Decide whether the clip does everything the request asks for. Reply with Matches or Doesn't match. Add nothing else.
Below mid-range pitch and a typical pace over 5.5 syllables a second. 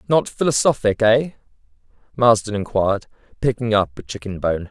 Doesn't match